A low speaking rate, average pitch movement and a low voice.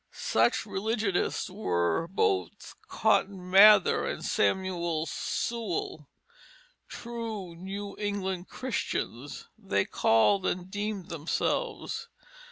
No: slow, 85 wpm; average, 3.8 semitones; high, 190 Hz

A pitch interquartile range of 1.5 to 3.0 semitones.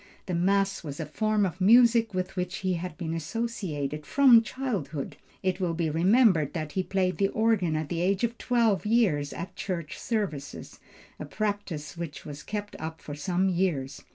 No: average, 5.0 semitones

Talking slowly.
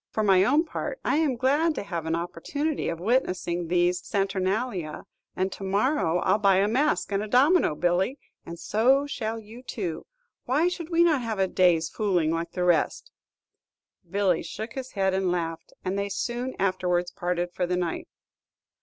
No: average, 180 wpm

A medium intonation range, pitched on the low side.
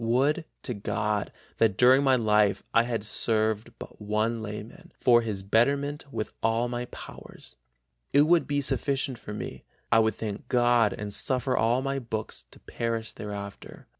Yes: average, 3.3 semitones; low, 115 Hz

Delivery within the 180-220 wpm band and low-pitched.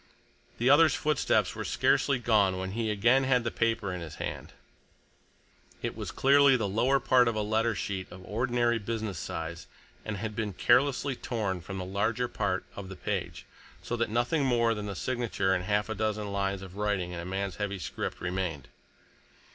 Yes: average, 185 wpm; low, 105 Hz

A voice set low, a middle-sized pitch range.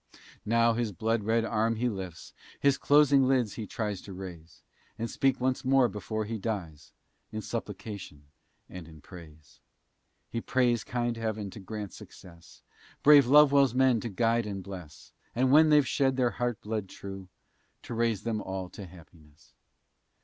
Yes: low, 110 Hz; average, 4.3 semitones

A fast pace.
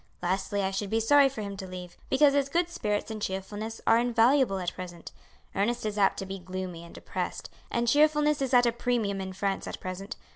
Yes: fast, 215 wpm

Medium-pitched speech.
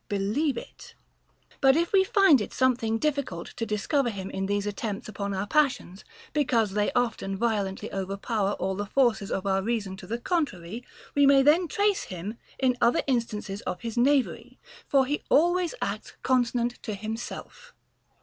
No: high, 230 Hz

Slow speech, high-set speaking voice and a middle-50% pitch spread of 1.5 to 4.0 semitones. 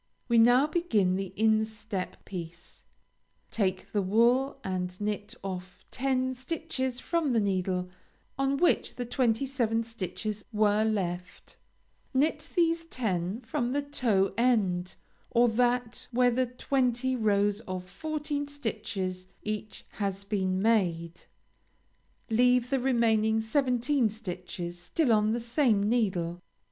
No: slow, 125 wpm; high, 220 Hz; average, 4.7 semitones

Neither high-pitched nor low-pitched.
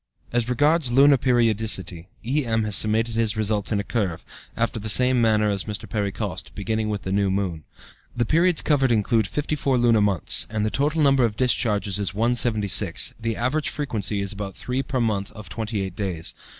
No: low, 110 Hz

